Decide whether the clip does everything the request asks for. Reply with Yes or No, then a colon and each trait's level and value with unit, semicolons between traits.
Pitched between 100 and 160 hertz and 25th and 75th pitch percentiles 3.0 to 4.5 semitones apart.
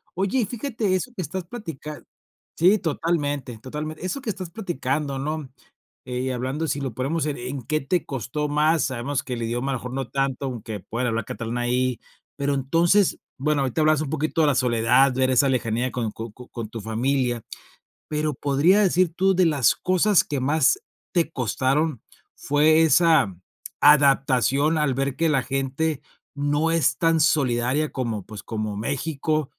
Yes: medium, 140 Hz; average, 4.0 semitones